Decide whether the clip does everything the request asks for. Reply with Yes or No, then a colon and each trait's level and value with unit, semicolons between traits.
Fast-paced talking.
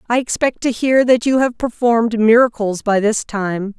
No: average, 190 wpm